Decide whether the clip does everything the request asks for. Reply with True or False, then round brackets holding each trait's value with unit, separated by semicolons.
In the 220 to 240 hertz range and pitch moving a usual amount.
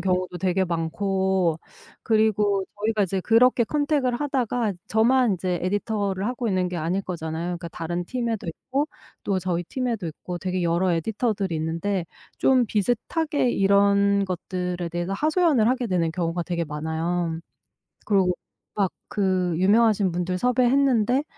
False (195 Hz; 4.5 semitones)